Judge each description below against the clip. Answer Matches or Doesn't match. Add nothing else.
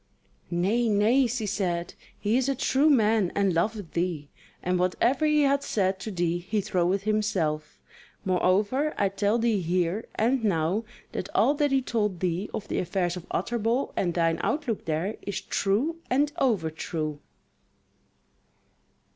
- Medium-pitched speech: Doesn't match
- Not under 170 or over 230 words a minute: Doesn't match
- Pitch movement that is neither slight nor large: Matches